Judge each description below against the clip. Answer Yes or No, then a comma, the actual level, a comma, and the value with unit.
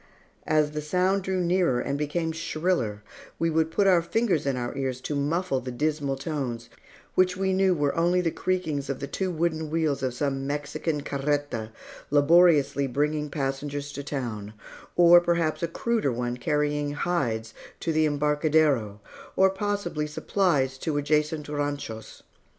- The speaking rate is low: No, average, 155 wpm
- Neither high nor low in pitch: Yes, medium, 150 Hz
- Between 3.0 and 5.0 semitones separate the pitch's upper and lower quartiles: Yes, average, 3.6 semitones